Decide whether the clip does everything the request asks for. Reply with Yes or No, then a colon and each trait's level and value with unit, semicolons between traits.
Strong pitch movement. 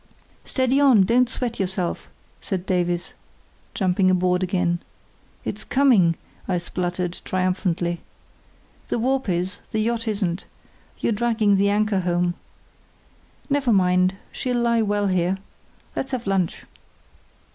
No: average, 4.4 semitones